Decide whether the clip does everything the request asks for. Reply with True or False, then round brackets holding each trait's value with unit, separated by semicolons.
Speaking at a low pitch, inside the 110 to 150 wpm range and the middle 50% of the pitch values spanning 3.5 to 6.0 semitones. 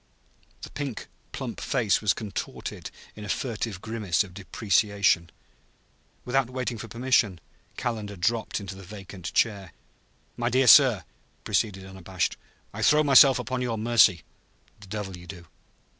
True (105 Hz; 145 wpm; 3.9 semitones)